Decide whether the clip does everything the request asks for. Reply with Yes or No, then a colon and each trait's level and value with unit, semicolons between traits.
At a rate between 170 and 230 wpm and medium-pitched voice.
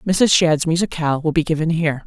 Yes: fast, 205 wpm; medium, 160 Hz